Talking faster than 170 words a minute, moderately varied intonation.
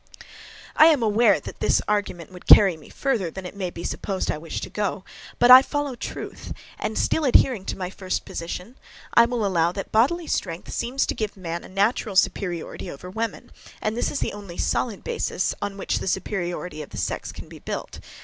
Yes: fast, 205 wpm; average, 4.7 semitones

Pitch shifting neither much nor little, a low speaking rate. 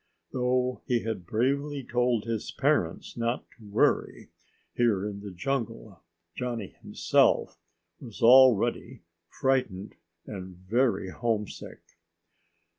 Yes: average, 3.6 semitones; slow, 105 wpm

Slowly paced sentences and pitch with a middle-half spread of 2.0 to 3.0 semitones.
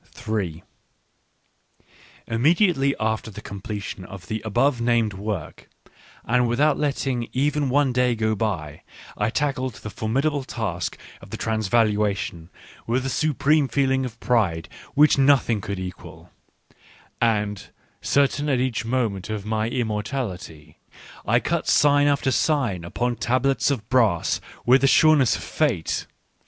No: slow, 130 wpm; average, 4.5 semitones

